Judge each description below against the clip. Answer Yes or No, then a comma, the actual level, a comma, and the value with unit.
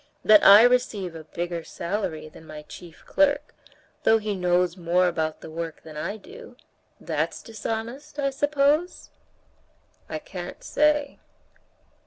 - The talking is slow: Yes, slow, 130 wpm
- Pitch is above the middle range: Yes, high, 205 Hz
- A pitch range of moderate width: No, wide, 8.7 semitones